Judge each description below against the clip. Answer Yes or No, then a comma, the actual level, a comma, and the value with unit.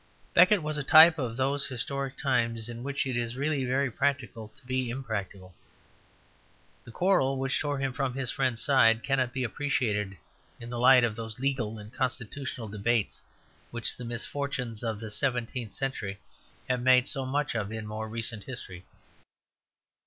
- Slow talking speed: No, average, 165 wpm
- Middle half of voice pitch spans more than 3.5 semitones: No, average, 3.1 semitones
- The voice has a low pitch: Yes, low, 125 Hz